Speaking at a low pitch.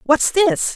No: very high, 315 Hz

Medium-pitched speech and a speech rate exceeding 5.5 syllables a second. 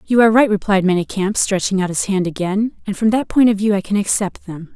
No: high, 200 Hz; 6.0 syllables/s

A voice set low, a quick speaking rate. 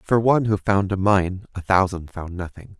Yes: very low, 95 Hz; fast, 235 wpm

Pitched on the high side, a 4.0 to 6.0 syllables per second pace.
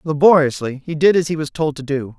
No: medium, 150 Hz; 5.8 syllables/s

